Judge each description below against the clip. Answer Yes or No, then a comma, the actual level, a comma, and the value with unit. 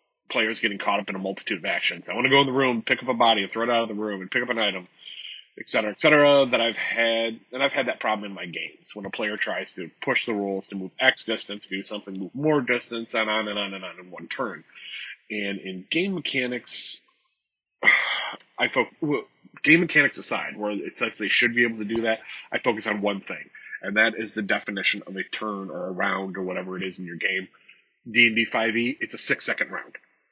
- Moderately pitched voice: No, low, 110 Hz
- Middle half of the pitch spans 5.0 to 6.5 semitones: No, average, 3.5 semitones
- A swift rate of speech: Yes, fast, 245 wpm